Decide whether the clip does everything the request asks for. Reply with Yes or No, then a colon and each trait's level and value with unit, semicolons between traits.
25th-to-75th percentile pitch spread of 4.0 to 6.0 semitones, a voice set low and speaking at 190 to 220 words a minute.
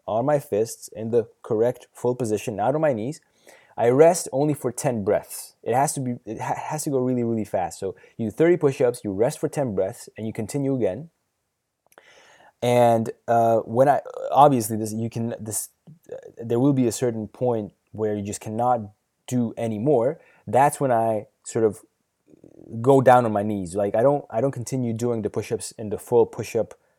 Yes: average, 4.3 semitones; low, 120 Hz; average, 200 wpm